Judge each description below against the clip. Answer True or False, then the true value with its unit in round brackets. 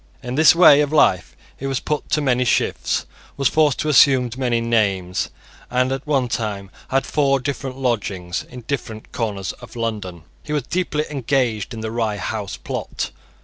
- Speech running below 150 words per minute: False (175 wpm)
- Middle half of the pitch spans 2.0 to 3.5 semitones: False (4.1 semitones)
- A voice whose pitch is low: True (125 Hz)